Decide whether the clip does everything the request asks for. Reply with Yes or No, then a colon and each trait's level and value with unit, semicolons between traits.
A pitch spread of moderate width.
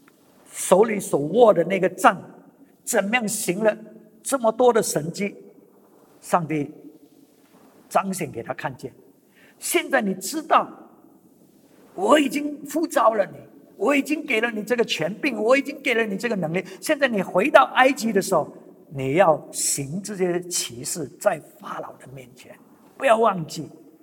No: wide, 7.0 semitones